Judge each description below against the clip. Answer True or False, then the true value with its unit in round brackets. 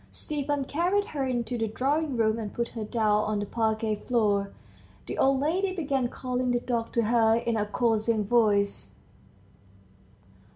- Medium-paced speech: True (160 wpm)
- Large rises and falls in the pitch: False (3.6 semitones)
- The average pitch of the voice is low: False (235 Hz)